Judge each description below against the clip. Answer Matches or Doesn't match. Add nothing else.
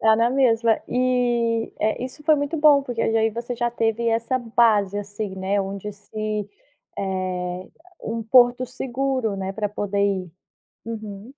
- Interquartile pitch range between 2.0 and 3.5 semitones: Matches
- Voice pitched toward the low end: Doesn't match